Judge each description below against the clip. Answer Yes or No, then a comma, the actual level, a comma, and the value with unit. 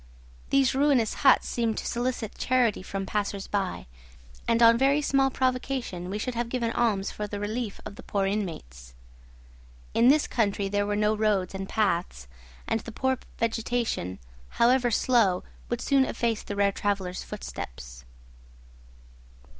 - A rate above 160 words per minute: No, average, 150 wpm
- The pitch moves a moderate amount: Yes, average, 3.9 semitones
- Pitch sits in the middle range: No, high, 215 Hz